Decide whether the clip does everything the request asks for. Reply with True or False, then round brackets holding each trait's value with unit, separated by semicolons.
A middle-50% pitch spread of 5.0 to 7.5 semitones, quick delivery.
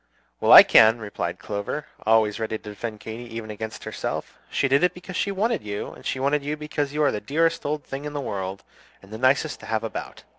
True (5.6 semitones; 230 wpm)